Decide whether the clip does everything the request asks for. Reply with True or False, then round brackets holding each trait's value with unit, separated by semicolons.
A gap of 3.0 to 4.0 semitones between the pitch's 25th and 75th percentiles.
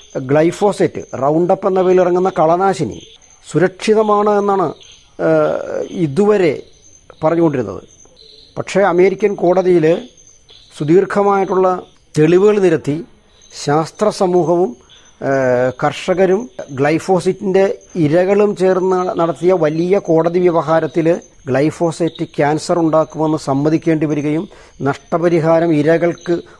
True (3.3 semitones)